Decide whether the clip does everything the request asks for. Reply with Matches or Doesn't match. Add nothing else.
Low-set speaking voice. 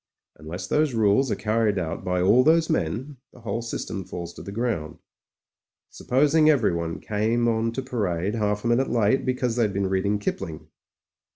Matches